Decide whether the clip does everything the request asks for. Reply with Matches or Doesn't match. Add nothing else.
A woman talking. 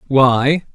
Doesn't match